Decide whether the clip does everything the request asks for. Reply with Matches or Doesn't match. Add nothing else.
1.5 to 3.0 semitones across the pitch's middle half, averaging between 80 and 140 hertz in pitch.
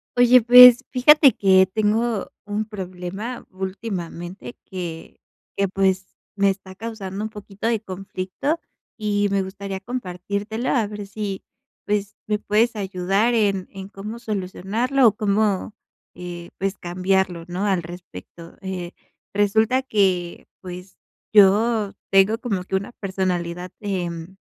Doesn't match